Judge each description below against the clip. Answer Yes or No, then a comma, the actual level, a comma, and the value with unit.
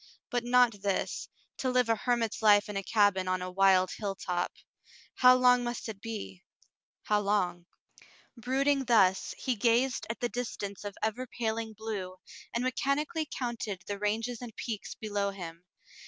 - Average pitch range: Yes, average, 3.7 semitones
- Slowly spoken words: No, average, 160 wpm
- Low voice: No, high, 220 Hz